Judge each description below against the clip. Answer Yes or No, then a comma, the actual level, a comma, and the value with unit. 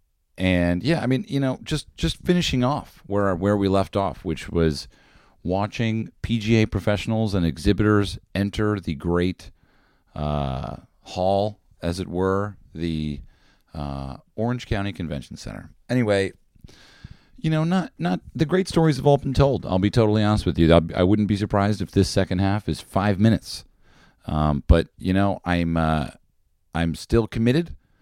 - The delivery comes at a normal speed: Yes, average, 160 wpm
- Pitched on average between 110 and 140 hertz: No, low, 100 Hz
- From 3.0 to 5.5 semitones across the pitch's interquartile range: Yes, average, 4.9 semitones